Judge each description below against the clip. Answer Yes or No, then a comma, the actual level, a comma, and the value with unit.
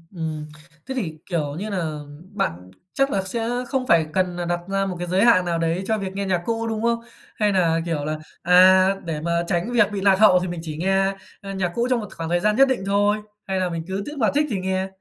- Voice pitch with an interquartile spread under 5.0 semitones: Yes, average, 3.5 semitones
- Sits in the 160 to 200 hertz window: Yes, high, 190 Hz